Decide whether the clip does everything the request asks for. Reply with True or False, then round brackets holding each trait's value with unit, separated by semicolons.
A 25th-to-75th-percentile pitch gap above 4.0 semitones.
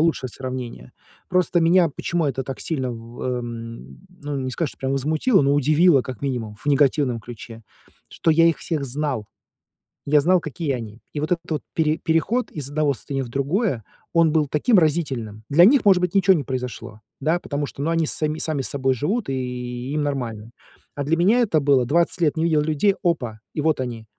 True (4.6 semitones)